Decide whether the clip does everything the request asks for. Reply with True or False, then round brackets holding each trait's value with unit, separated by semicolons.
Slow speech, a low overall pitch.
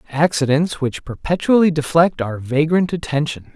False (120 wpm; 150 Hz)